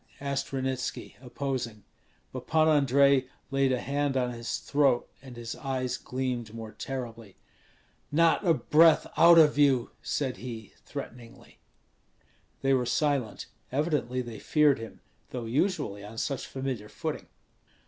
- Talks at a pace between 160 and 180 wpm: No, slow, 135 wpm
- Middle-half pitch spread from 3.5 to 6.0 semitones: No, average, 2.9 semitones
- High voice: No, low, 130 Hz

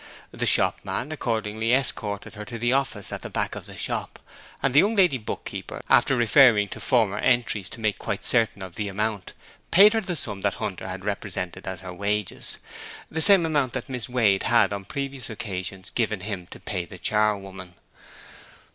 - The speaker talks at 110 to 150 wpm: No, average, 190 wpm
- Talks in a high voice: No, low, 110 Hz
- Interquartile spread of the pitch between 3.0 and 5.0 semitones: Yes, average, 4.5 semitones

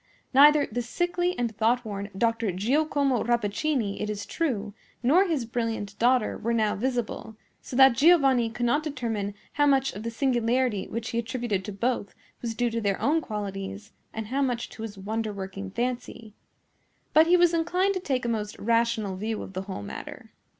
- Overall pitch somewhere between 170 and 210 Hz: No, high, 235 Hz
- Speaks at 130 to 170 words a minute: No, average, 180 wpm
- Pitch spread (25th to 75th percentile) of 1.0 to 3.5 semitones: No, average, 4.2 semitones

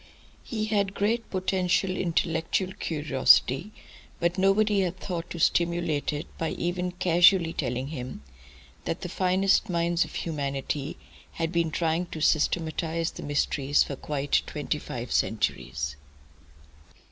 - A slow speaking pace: Yes, slow, 125 wpm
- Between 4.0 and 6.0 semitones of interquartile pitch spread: No, average, 3.6 semitones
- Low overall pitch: No, medium, 170 Hz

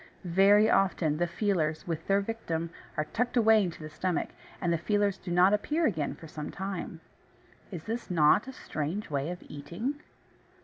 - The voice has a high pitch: No, medium, 180 Hz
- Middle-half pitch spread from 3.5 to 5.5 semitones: Yes, average, 4.6 semitones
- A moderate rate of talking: Yes, average, 175 wpm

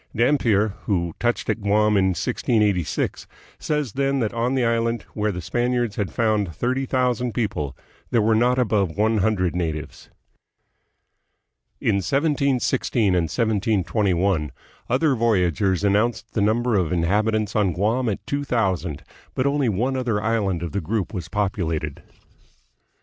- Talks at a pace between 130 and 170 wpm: Yes, average, 140 wpm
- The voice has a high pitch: No, low, 110 Hz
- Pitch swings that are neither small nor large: Yes, average, 4.2 semitones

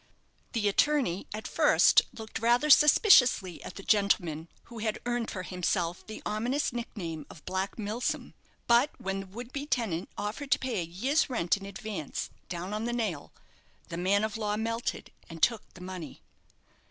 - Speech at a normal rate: Yes, average, 170 wpm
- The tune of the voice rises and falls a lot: No, average, 4.4 semitones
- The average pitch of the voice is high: Yes, high, 210 Hz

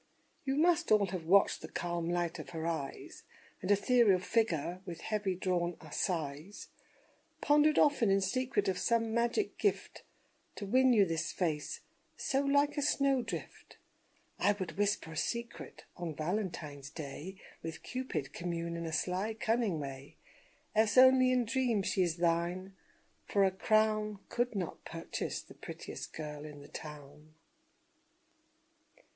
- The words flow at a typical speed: Yes, average, 145 wpm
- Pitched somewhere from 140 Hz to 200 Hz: Yes, high, 190 Hz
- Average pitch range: No, wide, 5.8 semitones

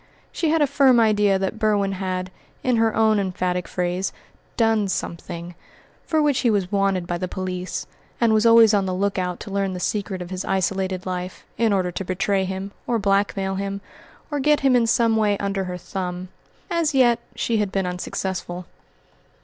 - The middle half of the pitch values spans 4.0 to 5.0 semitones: No, average, 3.3 semitones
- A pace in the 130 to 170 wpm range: No, average, 190 wpm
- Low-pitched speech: No, high, 195 Hz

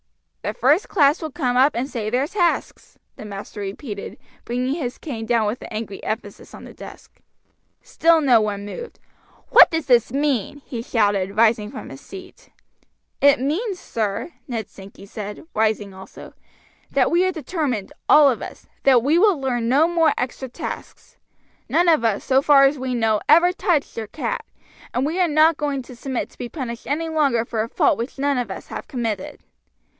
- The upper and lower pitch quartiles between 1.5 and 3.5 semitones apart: No, wide, 5.4 semitones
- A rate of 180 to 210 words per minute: Yes, average, 185 wpm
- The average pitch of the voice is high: Yes, very high, 255 Hz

